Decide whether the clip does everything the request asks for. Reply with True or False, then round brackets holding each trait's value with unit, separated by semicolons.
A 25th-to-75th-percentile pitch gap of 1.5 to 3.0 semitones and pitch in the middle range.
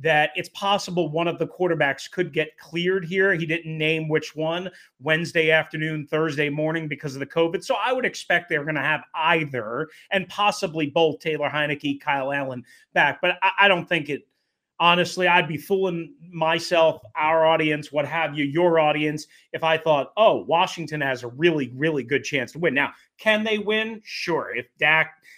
True (2.5 semitones; 160 Hz)